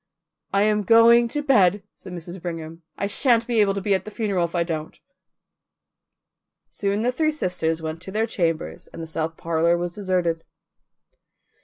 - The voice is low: No, medium, 185 Hz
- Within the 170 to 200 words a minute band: Yes, average, 175 wpm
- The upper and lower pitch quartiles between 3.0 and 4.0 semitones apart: No, average, 4.4 semitones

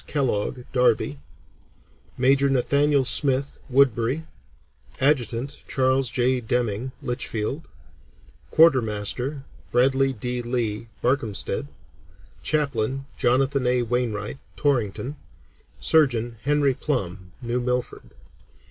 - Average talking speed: No, slow, 85 wpm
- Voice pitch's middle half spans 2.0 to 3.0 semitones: Yes, narrow, 2.6 semitones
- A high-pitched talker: No, low, 125 Hz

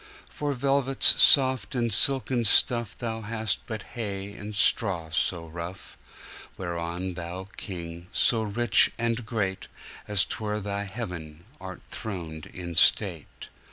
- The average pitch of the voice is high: No, low, 100 Hz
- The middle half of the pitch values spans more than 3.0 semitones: Yes, average, 4.8 semitones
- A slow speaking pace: Yes, slow, 115 wpm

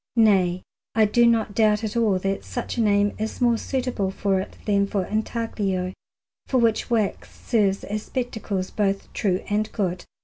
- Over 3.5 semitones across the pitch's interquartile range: No, average, 2.7 semitones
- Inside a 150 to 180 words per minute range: Yes, average, 170 wpm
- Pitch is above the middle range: Yes, high, 210 Hz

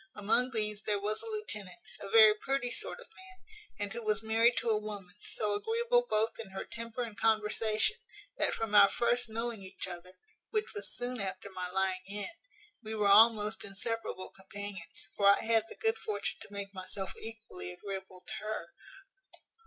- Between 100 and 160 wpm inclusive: No, average, 180 wpm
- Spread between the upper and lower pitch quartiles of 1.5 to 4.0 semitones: Yes, average, 2.7 semitones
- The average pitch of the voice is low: No, high, 215 Hz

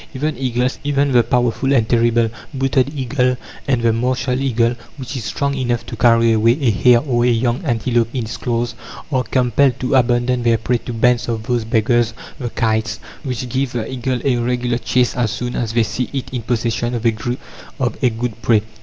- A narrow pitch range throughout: Yes, narrow, 1.7 semitones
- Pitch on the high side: No, low, 120 Hz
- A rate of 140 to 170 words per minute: No, average, 195 wpm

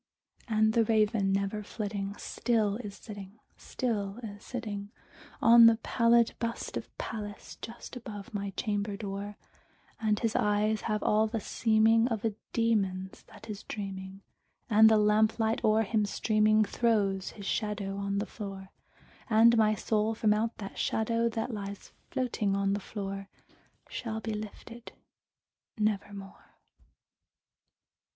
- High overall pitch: Yes, high, 215 Hz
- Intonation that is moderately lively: No, narrow, 1.9 semitones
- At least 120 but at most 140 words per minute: Yes, slow, 135 wpm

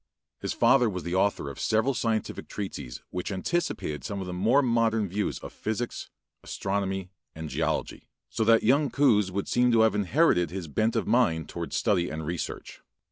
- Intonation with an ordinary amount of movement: Yes, average, 4.4 semitones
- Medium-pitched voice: No, low, 100 Hz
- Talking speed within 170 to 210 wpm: Yes, average, 180 wpm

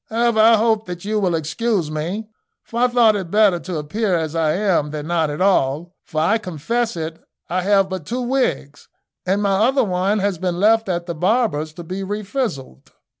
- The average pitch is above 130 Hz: Yes, high, 190 Hz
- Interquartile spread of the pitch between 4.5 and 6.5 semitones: Yes, average, 4.9 semitones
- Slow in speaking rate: No, average, 200 wpm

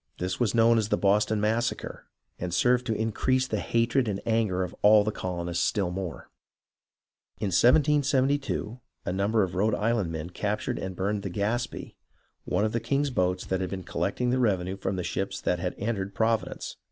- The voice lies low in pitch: Yes, low, 105 Hz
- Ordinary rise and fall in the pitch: Yes, average, 3.9 semitones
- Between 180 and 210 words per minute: Yes, average, 185 wpm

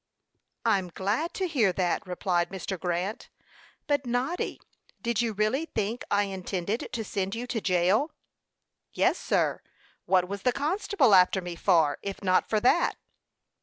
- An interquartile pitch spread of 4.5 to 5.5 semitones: Yes, average, 4.9 semitones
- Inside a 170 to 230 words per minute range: No, average, 150 wpm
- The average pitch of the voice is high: Yes, high, 205 Hz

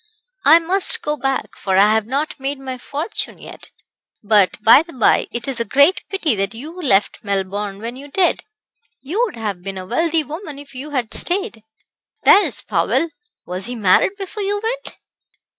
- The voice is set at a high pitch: Yes, very high, 270 Hz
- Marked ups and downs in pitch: Yes, wide, 7.5 semitones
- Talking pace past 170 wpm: Yes, average, 180 wpm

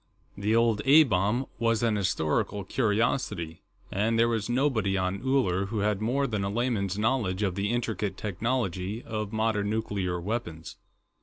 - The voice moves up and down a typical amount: Yes, average, 3.0 semitones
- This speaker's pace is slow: No, average, 155 wpm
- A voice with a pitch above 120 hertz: No, low, 105 Hz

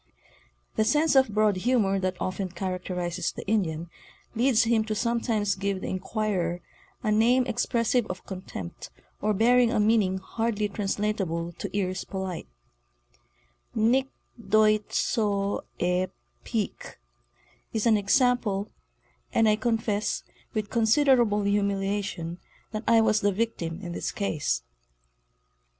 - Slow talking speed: Yes, slow, 125 wpm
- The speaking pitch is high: Yes, high, 210 Hz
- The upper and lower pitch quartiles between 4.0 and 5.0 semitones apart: No, average, 3.2 semitones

